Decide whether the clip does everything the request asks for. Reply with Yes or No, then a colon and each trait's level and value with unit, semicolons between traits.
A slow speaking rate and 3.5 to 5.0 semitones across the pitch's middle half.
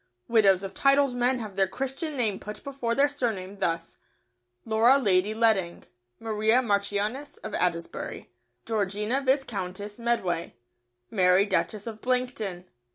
Yes: slow, 125 wpm; average, 4.3 semitones